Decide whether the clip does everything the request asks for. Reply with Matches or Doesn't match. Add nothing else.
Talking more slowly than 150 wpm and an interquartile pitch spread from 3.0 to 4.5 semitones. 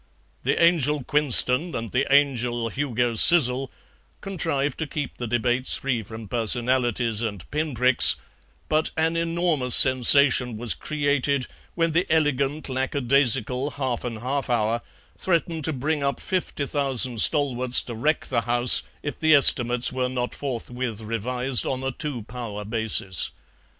Matches